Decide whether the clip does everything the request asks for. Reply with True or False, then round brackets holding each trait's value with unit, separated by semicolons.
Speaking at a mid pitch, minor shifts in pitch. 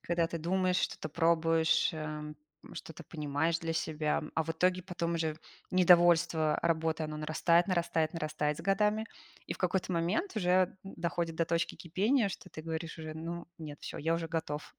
True (165 Hz; 1.9 semitones)